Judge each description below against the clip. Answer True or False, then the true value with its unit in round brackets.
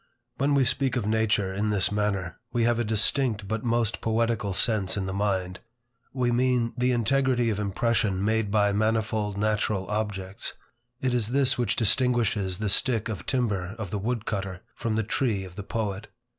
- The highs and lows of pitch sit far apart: False (3.0 semitones)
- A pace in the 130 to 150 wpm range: False (180 wpm)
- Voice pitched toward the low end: True (110 Hz)